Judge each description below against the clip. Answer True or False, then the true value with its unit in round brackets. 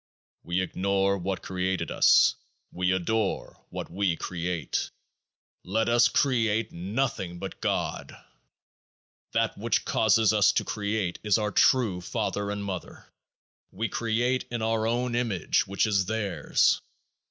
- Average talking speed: False (130 wpm)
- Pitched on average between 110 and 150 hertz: False (100 Hz)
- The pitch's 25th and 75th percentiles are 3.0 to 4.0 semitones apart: True (3.3 semitones)